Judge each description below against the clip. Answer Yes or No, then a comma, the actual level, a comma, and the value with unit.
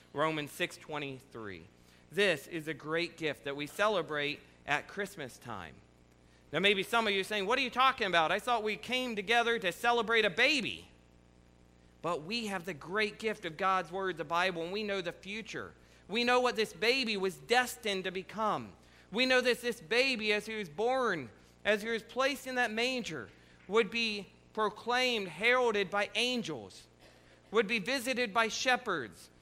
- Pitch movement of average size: No, wide, 6.2 semitones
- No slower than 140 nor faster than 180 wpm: Yes, average, 175 wpm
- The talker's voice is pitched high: Yes, high, 205 Hz